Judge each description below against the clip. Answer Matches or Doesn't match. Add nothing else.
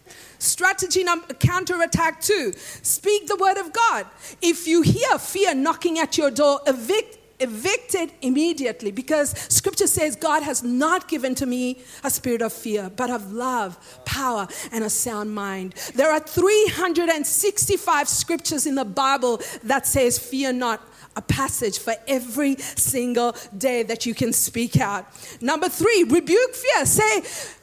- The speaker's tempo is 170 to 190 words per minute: Doesn't match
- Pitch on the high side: Matches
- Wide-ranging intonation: Matches